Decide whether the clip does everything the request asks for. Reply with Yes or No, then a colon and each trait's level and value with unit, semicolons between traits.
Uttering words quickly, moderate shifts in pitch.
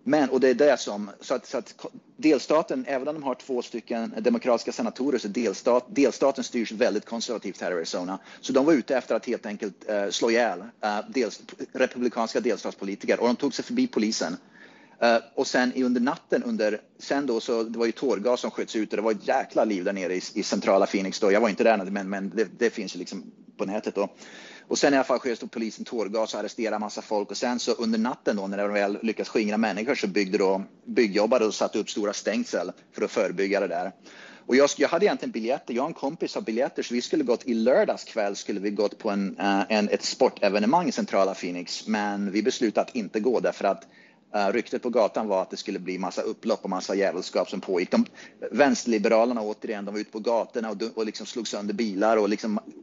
Yes: fast, 230 wpm; average, 3.2 semitones